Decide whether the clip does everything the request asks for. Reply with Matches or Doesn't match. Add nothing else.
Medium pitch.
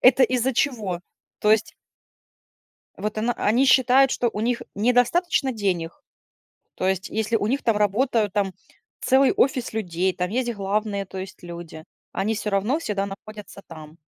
Doesn't match